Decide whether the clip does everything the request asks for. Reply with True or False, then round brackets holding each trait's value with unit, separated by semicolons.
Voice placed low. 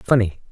True (105 Hz)